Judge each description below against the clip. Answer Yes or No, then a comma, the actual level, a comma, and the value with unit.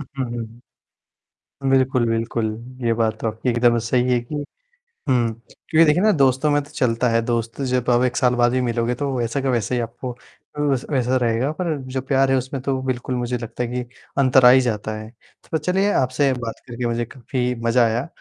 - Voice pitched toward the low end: Yes, low, 125 Hz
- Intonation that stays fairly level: Yes, narrow, 2.2 semitones